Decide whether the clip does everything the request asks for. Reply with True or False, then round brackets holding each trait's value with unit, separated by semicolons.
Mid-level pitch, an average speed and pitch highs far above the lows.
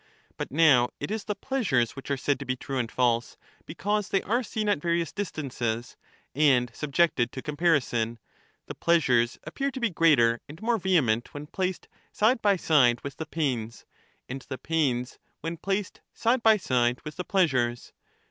True (150 Hz; 175 wpm; 7.5 semitones)